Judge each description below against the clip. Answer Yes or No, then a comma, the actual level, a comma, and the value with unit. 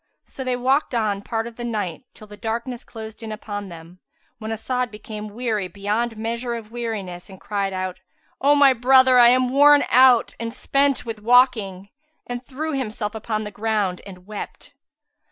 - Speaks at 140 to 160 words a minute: No, average, 175 wpm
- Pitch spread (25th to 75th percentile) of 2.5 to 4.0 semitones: Yes, average, 3.2 semitones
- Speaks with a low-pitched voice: No, high, 225 Hz